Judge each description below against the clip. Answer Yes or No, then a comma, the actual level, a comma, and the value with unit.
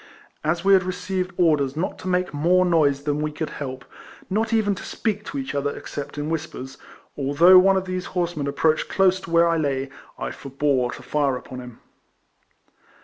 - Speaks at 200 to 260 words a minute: No, average, 190 wpm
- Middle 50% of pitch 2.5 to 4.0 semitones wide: No, average, 4.5 semitones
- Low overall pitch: No, medium, 160 Hz